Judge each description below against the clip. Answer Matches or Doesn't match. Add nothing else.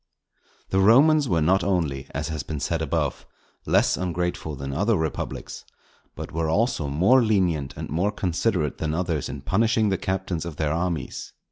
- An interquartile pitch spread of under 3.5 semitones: Doesn't match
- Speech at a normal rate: Matches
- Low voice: Matches